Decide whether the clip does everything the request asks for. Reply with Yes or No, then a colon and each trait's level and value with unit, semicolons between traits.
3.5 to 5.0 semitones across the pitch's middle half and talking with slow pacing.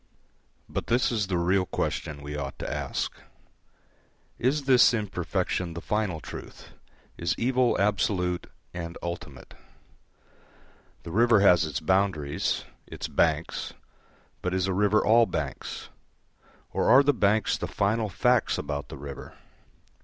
Yes: average, 4.6 semitones; slow, 130 wpm